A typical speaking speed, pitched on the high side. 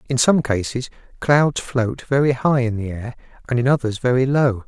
No: average, 190 wpm; low, 125 Hz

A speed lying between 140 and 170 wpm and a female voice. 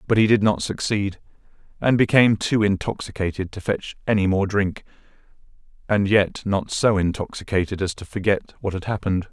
No: average, 160 wpm; male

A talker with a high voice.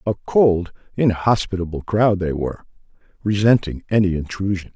No: very low, 95 Hz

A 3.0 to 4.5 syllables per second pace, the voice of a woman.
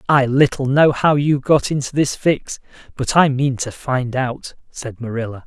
No: 4.4 syllables/s; male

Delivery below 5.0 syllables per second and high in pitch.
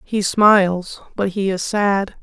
Yes: 3.6 syllables/s; high, 195 Hz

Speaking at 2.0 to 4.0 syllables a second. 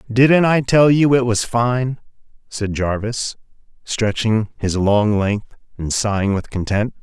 Yes: 3.8 syllables/s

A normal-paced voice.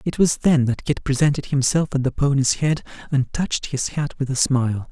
No: fast, 220 wpm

